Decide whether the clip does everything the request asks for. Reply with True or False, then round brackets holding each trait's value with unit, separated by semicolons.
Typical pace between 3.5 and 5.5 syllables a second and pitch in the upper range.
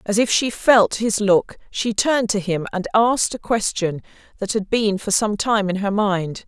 True (4.6 syllables/s; 210 Hz)